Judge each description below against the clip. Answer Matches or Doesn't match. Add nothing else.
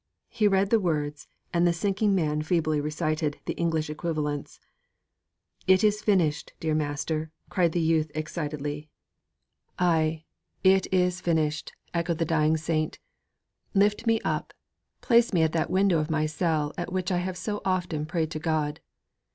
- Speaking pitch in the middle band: Matches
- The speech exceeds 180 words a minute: Doesn't match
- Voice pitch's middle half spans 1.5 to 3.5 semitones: Matches